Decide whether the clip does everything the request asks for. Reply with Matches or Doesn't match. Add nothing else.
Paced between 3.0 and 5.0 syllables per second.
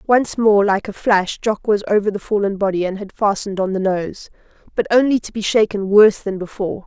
Doesn't match